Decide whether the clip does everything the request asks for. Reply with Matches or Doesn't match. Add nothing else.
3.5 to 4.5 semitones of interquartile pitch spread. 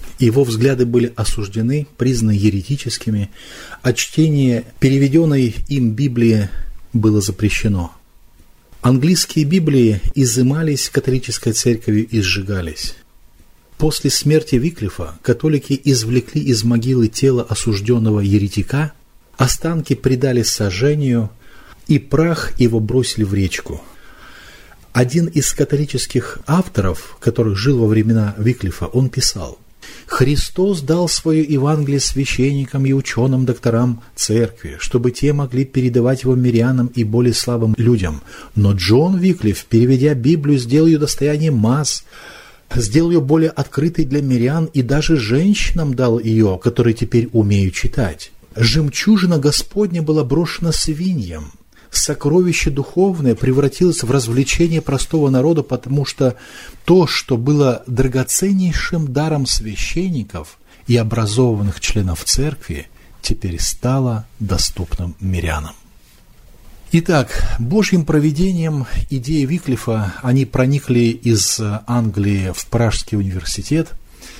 Doesn't match